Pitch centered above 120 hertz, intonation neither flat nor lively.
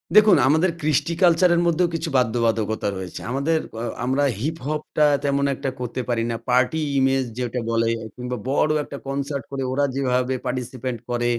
Yes: low, 135 Hz; average, 3.8 semitones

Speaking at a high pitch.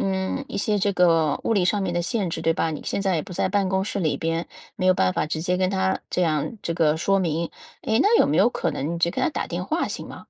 No: medium, 180 Hz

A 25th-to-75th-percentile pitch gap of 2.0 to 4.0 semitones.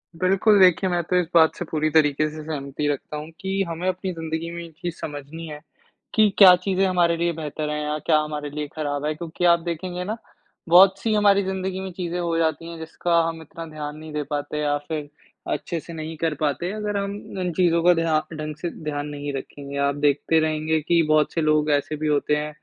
Yes: average, 2.8 semitones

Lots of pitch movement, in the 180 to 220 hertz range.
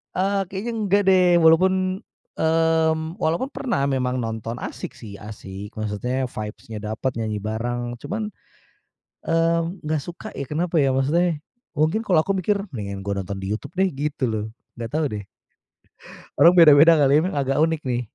No: wide, 6.9 semitones; medium, 145 Hz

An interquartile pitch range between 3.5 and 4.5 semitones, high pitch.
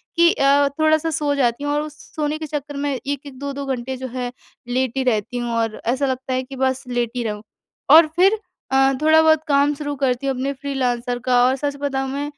No: narrow, 2.4 semitones; very high, 275 Hz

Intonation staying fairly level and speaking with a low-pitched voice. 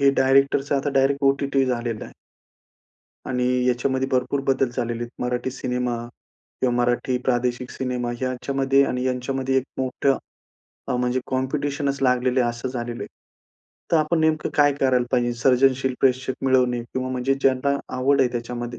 Yes: narrow, 1.7 semitones; low, 130 Hz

